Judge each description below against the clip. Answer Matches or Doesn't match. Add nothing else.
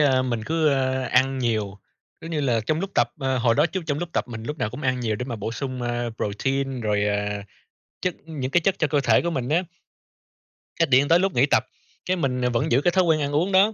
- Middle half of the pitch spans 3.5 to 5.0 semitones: Matches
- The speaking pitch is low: Matches